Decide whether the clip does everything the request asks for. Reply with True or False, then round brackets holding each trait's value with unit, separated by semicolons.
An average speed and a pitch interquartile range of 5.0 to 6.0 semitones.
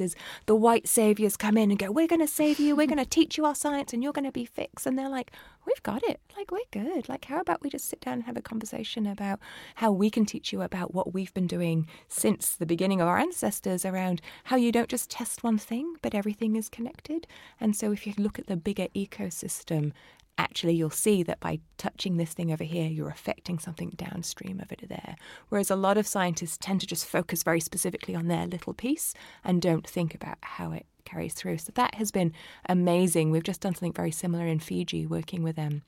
False (235 wpm; 5.6 semitones)